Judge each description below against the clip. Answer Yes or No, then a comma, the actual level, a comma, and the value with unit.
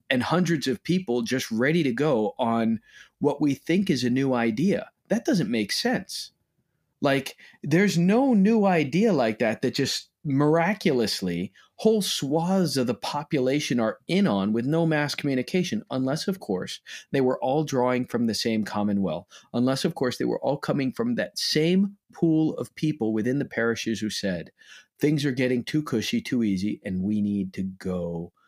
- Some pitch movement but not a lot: No, wide, 6.2 semitones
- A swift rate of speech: No, average, 175 wpm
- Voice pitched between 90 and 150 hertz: Yes, medium, 140 Hz